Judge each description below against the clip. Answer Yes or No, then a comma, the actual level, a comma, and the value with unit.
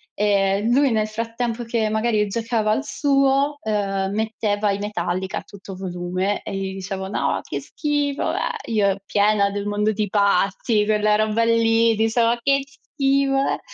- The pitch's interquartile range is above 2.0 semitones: Yes, narrow, 2.6 semitones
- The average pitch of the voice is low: No, high, 215 Hz